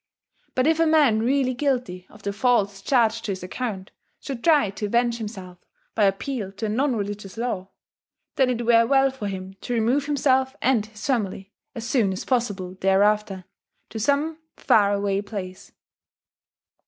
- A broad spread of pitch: No, average, 4.4 semitones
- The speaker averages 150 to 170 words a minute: Yes, average, 165 wpm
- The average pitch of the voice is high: Yes, high, 225 Hz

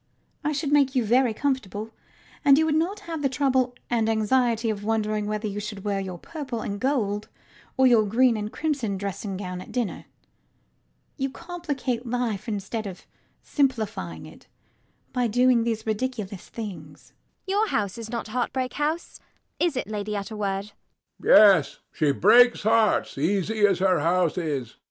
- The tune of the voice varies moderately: Yes, average, 4.3 semitones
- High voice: Yes, high, 225 Hz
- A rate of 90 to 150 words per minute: No, average, 160 wpm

